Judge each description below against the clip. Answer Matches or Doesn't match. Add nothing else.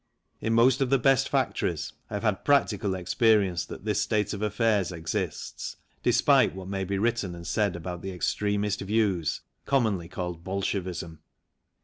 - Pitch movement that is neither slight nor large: Matches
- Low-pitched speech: Matches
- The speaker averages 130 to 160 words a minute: Matches